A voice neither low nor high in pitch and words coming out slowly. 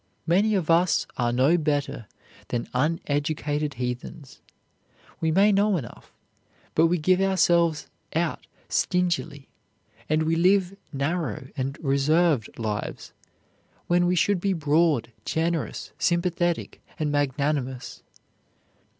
Yes: medium, 160 Hz; slow, 110 wpm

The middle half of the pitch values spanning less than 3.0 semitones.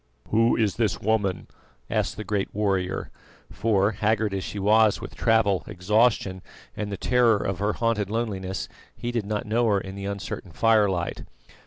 Yes: narrow, 2.4 semitones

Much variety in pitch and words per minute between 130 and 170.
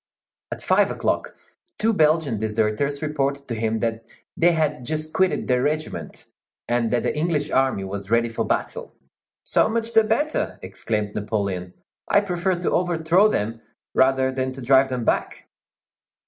Yes: wide, 6.1 semitones; average, 155 wpm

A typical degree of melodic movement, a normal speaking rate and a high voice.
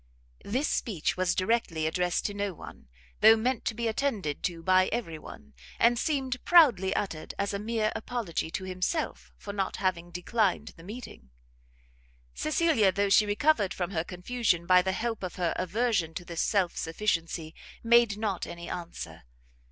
Yes: average, 4.6 semitones; average, 165 wpm; high, 195 Hz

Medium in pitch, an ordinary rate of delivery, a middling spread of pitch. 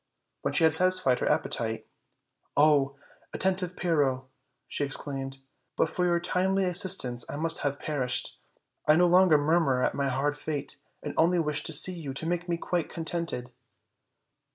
Yes: medium, 155 Hz; average, 165 wpm; average, 4.1 semitones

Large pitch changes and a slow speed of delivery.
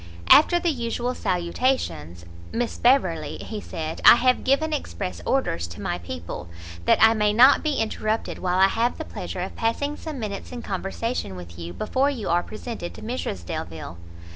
No: wide, 8.3 semitones; average, 175 wpm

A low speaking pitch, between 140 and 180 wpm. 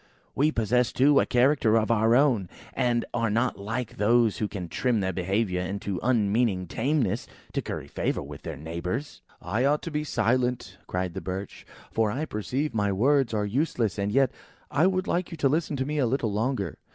No: low, 115 Hz; average, 200 wpm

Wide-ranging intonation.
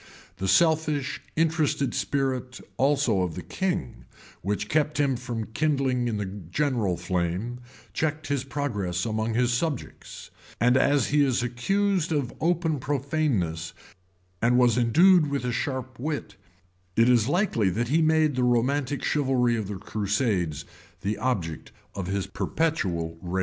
Yes: wide, 5.9 semitones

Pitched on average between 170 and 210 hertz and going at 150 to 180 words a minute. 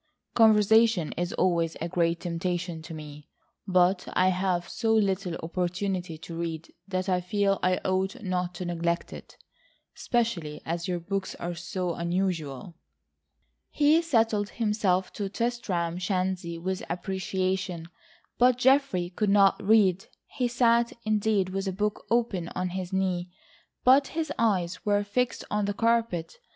No: medium, 185 Hz; average, 140 wpm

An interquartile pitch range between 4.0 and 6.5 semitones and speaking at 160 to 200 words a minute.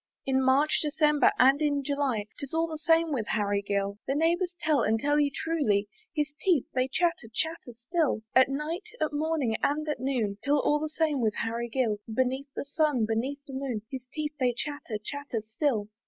Yes: average, 4.4 semitones; average, 195 wpm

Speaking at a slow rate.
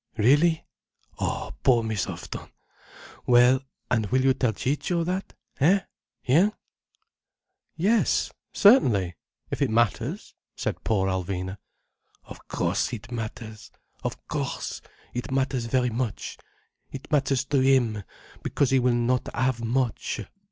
Yes: slow, 115 wpm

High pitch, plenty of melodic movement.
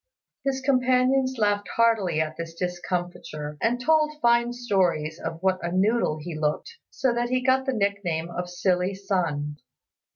Yes: high, 195 Hz; wide, 6.3 semitones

